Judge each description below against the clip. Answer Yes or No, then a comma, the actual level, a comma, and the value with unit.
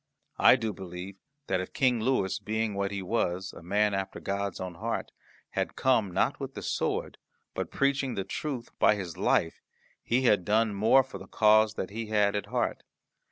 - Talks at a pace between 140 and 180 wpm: No, average, 190 wpm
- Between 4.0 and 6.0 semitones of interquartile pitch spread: No, average, 3.0 semitones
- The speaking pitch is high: No, low, 105 Hz